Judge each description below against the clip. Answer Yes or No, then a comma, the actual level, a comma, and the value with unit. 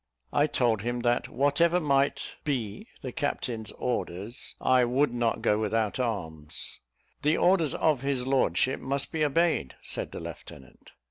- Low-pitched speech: Yes, low, 130 Hz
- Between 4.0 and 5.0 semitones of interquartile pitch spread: Yes, average, 4.3 semitones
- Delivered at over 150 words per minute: No, average, 145 wpm